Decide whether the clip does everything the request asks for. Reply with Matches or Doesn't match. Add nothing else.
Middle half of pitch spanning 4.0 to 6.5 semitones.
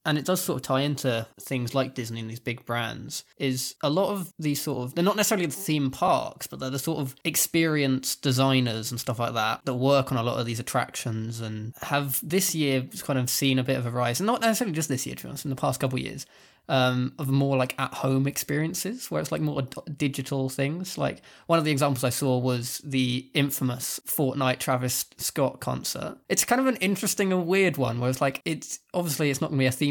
Doesn't match